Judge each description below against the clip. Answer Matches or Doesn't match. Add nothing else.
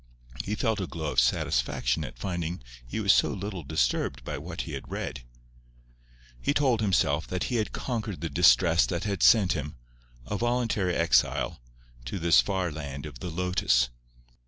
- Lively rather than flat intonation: Matches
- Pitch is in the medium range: Doesn't match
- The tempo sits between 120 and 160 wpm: Doesn't match